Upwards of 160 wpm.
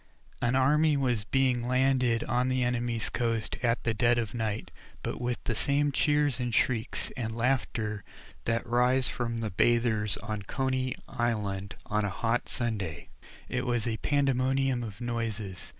No: average, 155 wpm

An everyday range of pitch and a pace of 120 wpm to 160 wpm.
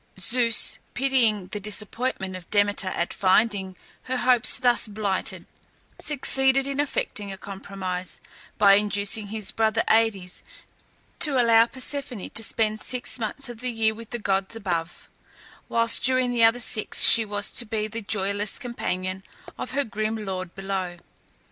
Yes: average, 3.6 semitones; average, 150 wpm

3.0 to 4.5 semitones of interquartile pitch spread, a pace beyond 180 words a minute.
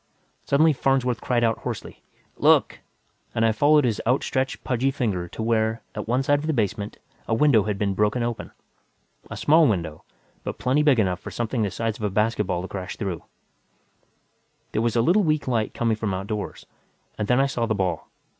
Yes: average, 3.9 semitones; average, 195 wpm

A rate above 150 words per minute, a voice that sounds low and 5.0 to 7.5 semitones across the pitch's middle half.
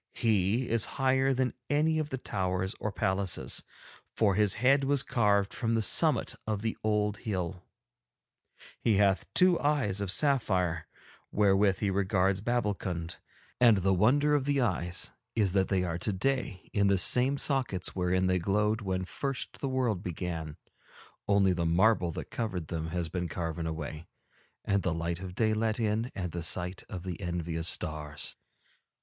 No: average, 165 wpm; low, 100 Hz; average, 4.3 semitones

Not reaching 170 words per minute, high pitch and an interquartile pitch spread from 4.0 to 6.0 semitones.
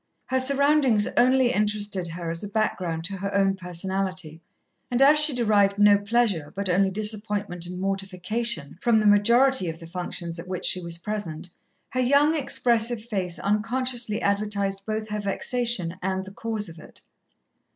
Yes: average, 160 wpm; high, 205 Hz; average, 4.3 semitones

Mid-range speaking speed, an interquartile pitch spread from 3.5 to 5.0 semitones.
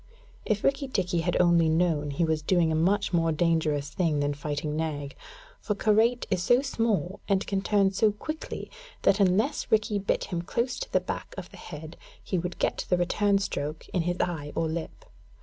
Yes: average, 195 wpm; average, 4.4 semitones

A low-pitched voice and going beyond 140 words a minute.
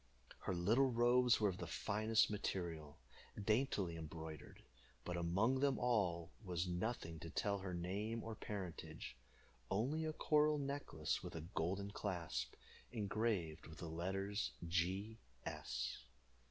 No: very low, 95 Hz; slow, 135 wpm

